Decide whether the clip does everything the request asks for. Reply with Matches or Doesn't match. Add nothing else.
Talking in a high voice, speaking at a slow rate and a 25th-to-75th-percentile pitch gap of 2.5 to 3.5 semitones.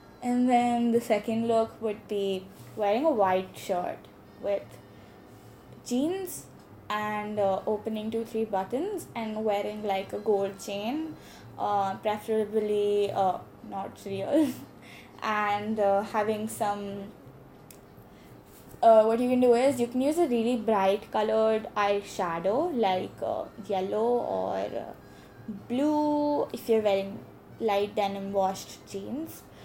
Matches